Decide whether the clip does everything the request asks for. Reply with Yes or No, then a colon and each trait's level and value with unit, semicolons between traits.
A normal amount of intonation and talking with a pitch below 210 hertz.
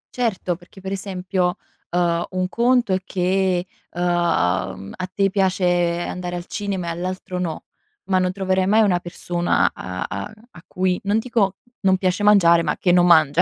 No: narrow, 1.7 semitones; medium, 185 Hz